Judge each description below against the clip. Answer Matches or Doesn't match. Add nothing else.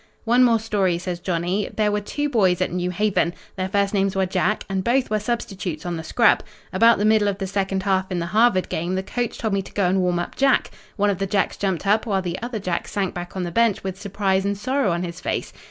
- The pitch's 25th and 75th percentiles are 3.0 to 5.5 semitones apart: Doesn't match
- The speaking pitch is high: Matches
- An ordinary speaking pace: Doesn't match